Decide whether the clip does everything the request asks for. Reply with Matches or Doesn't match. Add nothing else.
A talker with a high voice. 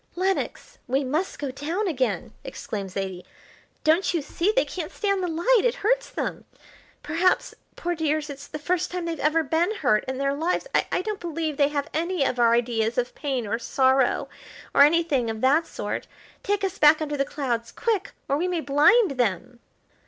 Matches